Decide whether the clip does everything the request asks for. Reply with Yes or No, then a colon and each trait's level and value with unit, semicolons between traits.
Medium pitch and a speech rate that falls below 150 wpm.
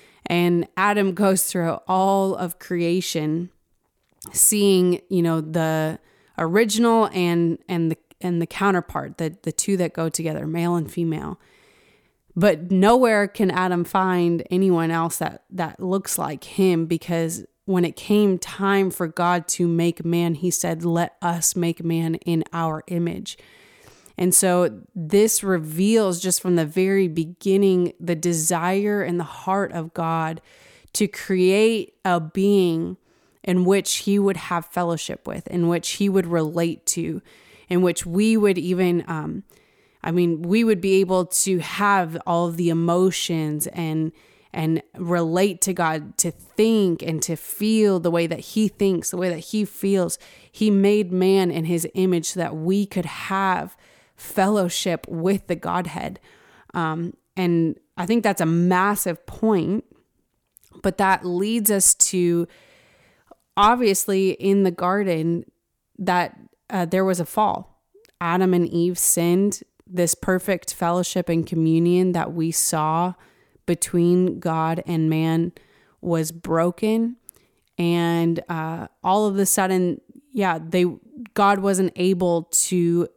Yes: medium, 180 Hz; average, 140 wpm